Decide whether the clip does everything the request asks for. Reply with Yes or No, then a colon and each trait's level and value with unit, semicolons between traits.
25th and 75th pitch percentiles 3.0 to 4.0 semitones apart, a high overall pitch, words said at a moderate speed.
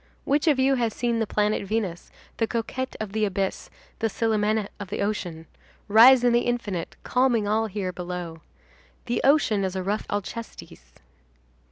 Yes: average, 3.5 semitones; high, 215 Hz; average, 165 wpm